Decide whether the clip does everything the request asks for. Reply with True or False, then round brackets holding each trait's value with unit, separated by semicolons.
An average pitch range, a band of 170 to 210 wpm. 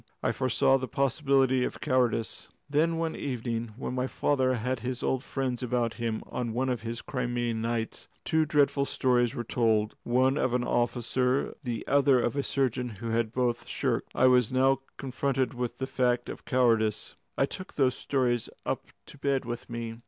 False (2.1 semitones; 180 wpm)